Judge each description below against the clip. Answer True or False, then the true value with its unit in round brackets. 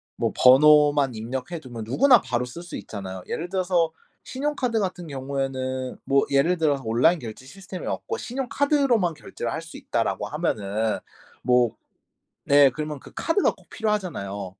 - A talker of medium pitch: True (145 Hz)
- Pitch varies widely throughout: True (6.4 semitones)